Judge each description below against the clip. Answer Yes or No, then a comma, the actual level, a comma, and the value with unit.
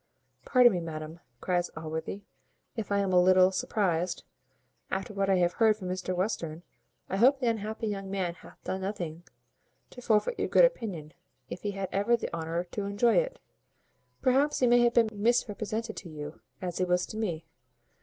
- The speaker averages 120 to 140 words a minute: No, average, 185 wpm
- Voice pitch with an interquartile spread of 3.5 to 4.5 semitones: Yes, average, 4.1 semitones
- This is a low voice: No, high, 195 Hz